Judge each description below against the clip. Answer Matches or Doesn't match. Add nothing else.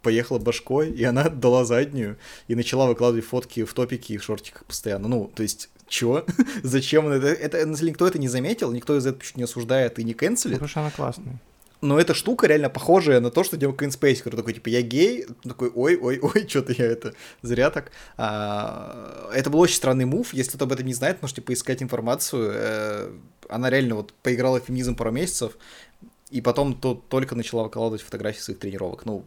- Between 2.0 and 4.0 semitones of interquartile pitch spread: Matches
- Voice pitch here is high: Doesn't match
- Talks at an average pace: Doesn't match